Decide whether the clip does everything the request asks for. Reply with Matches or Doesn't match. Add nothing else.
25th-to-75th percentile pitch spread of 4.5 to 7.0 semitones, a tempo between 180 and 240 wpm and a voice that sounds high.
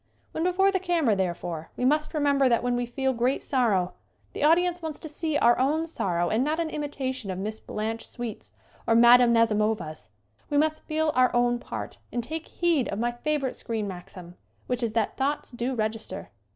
Matches